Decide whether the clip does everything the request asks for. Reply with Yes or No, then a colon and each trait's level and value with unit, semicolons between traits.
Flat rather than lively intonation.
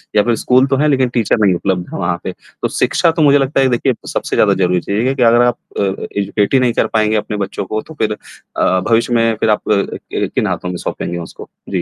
No: average, 4.3 semitones